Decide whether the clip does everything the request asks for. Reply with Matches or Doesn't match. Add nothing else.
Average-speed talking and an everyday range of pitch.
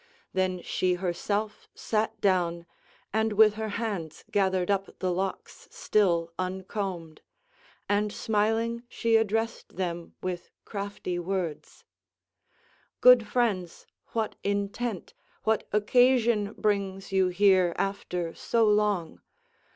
Doesn't match